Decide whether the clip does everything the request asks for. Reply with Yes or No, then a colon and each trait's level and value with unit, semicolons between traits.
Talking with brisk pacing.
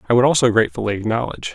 No: average, 195 wpm